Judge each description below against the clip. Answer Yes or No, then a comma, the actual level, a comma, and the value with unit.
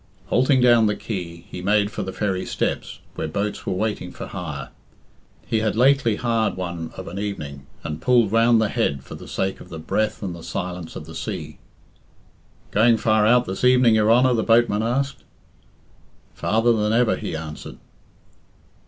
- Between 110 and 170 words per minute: No, average, 180 wpm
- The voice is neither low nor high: No, low, 105 Hz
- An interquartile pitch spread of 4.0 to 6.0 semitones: Yes, average, 4.3 semitones